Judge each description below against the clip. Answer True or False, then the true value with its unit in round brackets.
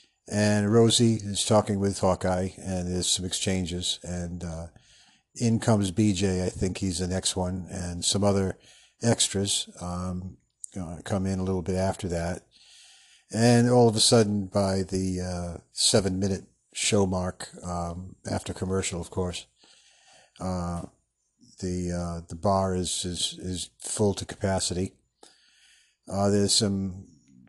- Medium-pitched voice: False (95 Hz)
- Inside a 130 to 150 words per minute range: True (140 wpm)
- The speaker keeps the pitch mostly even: True (1.9 semitones)